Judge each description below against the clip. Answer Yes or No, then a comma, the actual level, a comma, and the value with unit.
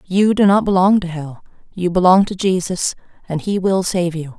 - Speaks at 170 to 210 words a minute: Yes, fast, 205 wpm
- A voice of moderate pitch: Yes, medium, 180 Hz